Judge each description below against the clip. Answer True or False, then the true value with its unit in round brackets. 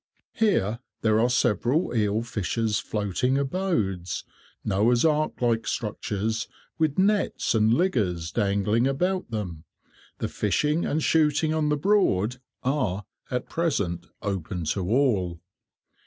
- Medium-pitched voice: False (115 Hz)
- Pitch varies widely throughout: True (6.8 semitones)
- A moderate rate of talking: False (120 wpm)